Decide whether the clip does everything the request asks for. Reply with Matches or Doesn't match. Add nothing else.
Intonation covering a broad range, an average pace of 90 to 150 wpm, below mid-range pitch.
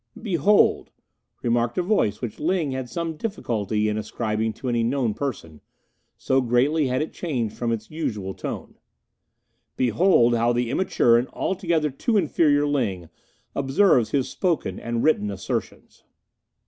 Matches